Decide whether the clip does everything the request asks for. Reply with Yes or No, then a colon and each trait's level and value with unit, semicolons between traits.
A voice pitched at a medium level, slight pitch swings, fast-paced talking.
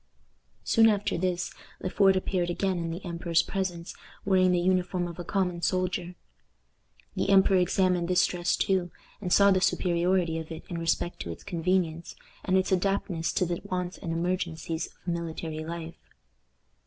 No: medium, 180 Hz; narrow, 1.7 semitones; average, 165 wpm